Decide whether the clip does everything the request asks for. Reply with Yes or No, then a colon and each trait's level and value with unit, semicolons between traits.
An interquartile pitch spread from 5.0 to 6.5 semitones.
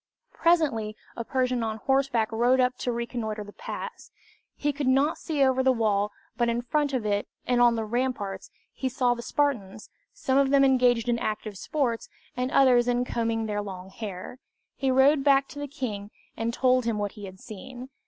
No: average, 3.3 semitones